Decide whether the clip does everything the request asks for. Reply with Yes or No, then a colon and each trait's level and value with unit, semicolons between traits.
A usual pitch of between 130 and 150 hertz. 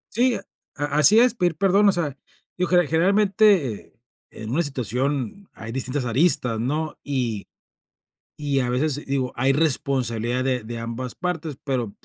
Yes: medium, 140 Hz